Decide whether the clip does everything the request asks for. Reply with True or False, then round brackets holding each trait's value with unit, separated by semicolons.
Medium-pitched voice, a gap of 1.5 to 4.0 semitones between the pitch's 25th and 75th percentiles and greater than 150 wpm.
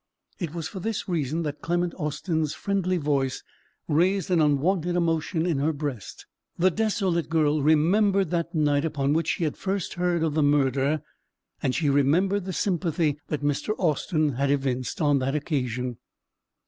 True (155 Hz; 3.6 semitones; 160 wpm)